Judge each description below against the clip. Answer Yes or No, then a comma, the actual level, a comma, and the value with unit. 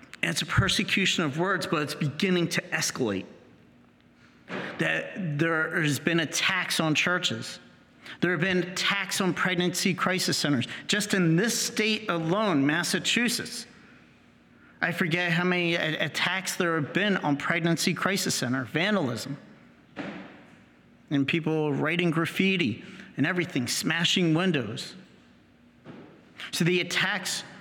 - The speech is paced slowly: Yes, slow, 120 wpm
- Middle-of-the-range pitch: Yes, medium, 175 Hz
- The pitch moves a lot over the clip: No, average, 3.3 semitones